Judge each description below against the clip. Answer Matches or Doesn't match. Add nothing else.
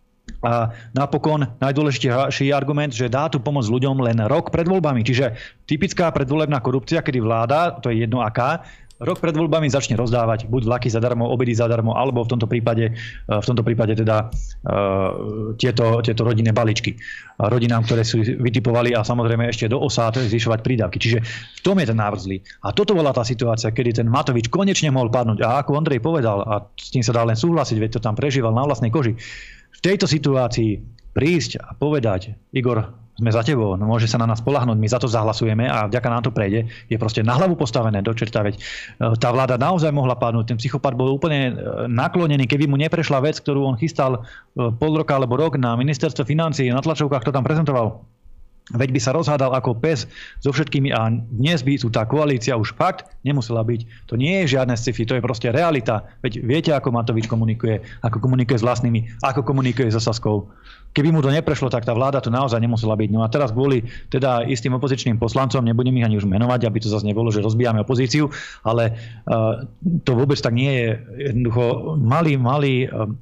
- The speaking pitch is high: Doesn't match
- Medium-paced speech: Doesn't match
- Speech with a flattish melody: Doesn't match